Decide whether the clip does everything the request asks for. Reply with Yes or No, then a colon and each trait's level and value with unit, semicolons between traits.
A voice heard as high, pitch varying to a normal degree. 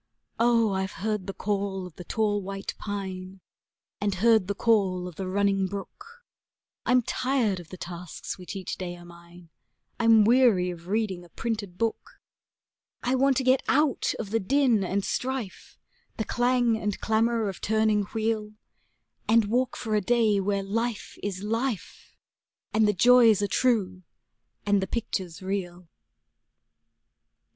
Yes: high, 205 Hz; average, 3.4 semitones